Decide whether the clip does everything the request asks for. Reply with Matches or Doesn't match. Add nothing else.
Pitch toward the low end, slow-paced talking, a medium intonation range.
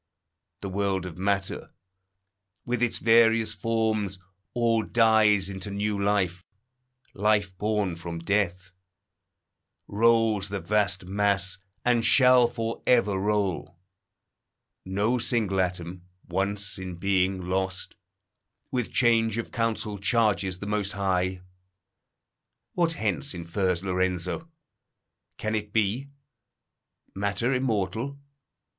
Matches